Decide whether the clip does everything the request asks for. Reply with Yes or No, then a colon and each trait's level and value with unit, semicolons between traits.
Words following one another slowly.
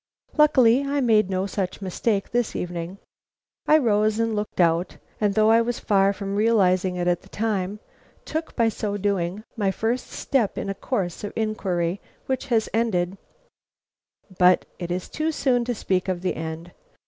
No: average, 170 wpm